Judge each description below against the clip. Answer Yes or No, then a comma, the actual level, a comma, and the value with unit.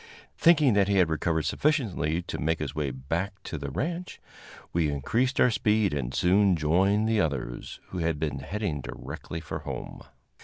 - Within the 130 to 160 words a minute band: No, average, 170 wpm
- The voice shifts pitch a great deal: Yes, wide, 5.8 semitones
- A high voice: No, very low, 85 Hz